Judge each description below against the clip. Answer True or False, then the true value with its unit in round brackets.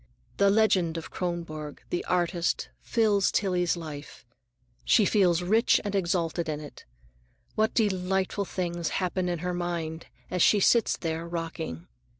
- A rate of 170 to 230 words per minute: False (140 wpm)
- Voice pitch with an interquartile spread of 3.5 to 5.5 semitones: False (2.8 semitones)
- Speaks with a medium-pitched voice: True (175 Hz)